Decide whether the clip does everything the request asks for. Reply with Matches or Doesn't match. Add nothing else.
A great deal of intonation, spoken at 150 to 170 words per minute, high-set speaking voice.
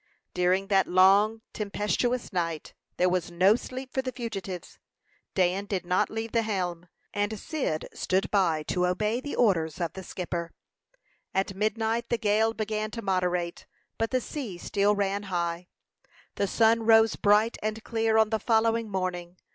Doesn't match